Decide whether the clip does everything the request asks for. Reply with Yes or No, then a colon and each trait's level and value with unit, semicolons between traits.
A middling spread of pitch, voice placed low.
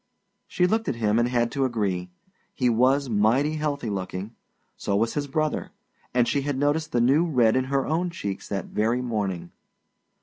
Yes: average, 4.9 semitones; low, 125 Hz